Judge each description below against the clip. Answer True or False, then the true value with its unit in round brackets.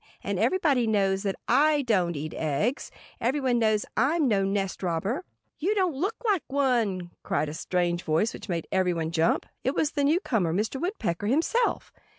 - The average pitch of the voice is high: True (220 Hz)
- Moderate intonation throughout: False (8.2 semitones)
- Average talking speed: True (165 wpm)